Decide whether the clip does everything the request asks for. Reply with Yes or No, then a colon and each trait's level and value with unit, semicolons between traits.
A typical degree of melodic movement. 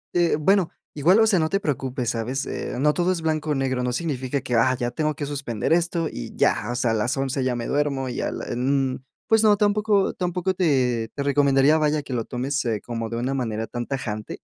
Yes: average, 4.5 semitones